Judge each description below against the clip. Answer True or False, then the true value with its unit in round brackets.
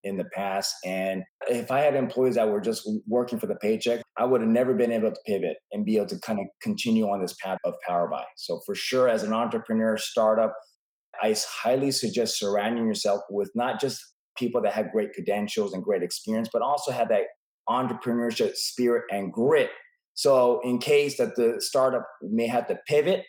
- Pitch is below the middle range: True (115 Hz)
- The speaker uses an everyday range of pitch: True (3.4 semitones)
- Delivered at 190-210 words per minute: True (200 wpm)